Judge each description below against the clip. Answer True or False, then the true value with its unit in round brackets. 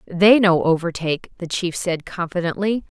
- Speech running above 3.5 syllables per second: True (5.0 syllables/s)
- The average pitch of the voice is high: False (180 Hz)